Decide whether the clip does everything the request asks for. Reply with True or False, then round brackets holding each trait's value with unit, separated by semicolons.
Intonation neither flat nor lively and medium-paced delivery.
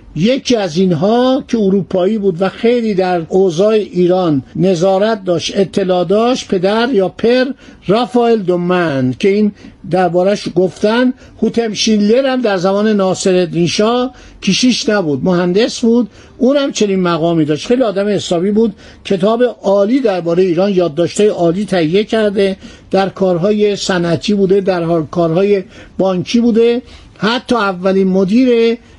True (3.9 semitones; 130 wpm)